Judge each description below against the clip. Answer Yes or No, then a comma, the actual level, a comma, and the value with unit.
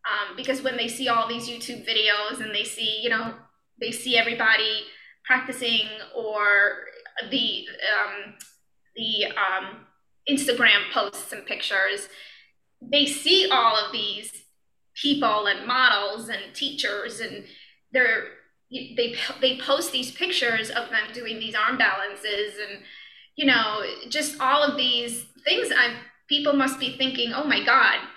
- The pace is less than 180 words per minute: Yes, average, 140 wpm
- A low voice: No, high, 235 Hz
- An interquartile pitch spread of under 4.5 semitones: Yes, average, 3.4 semitones